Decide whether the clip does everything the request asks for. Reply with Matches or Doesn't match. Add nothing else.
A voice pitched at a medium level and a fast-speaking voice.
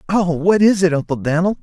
Matches